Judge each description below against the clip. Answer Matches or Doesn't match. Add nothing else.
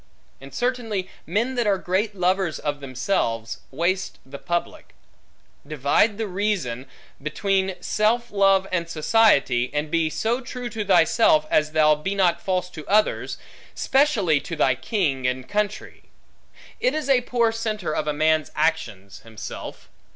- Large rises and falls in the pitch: Matches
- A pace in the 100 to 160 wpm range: Matches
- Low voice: Doesn't match